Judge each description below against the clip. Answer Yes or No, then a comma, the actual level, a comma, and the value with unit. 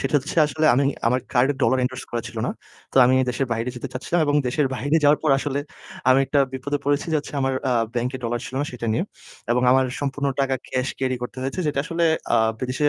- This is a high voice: No, low, 135 Hz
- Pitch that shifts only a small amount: Yes, narrow, 2.3 semitones